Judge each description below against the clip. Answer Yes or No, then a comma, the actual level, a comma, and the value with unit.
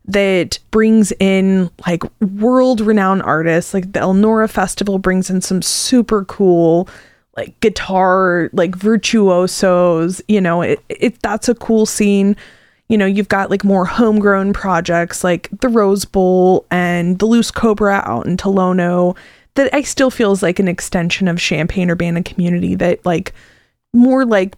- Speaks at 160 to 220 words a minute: No, average, 150 wpm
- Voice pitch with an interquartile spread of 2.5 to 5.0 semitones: Yes, average, 3.2 semitones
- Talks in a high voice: Yes, high, 195 Hz